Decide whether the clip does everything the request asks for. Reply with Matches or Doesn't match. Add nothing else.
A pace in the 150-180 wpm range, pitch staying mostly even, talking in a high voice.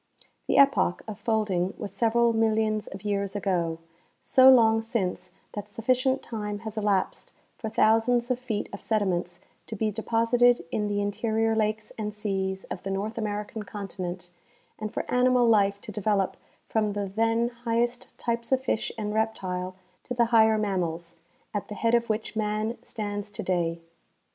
Matches